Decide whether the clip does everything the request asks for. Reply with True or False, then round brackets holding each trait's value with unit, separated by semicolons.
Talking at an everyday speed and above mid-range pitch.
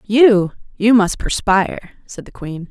True (155 wpm; 205 Hz)